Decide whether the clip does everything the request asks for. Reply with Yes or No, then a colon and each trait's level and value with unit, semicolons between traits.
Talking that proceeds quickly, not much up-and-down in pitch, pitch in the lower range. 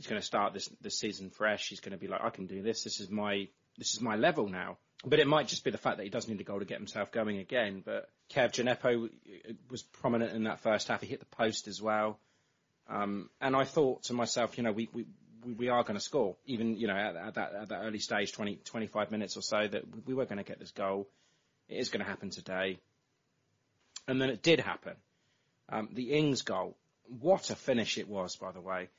No: fast, 245 wpm; average, 3.5 semitones; low, 115 Hz